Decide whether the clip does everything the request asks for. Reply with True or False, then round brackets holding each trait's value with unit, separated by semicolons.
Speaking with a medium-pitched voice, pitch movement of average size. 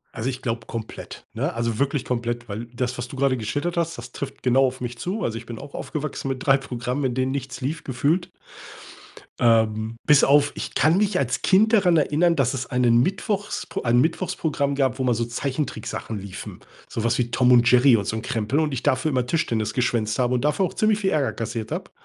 False (130 Hz; 3.9 semitones)